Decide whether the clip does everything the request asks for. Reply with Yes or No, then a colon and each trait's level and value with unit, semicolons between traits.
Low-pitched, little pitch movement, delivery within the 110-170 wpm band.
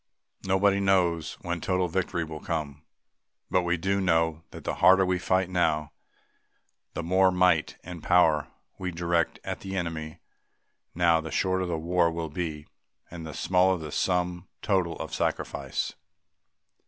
Yes: very low, 85 Hz; narrow, 2.1 semitones; average, 150 wpm